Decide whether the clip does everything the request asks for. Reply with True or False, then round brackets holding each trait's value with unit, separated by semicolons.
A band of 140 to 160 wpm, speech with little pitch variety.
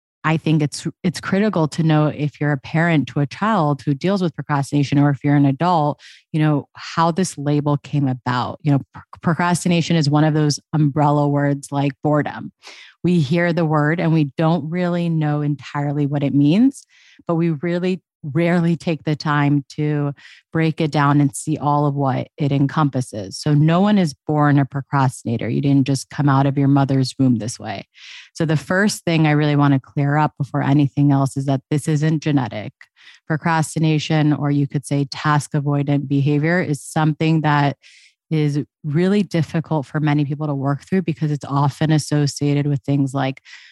False (185 wpm; 2.1 semitones)